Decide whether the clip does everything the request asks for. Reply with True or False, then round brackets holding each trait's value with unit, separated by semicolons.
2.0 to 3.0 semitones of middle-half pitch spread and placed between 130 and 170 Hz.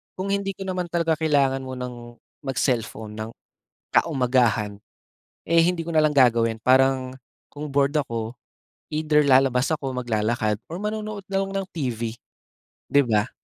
False (5.6 semitones; 135 Hz)